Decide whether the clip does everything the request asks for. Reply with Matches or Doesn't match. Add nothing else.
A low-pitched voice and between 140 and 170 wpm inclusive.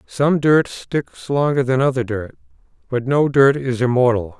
Matches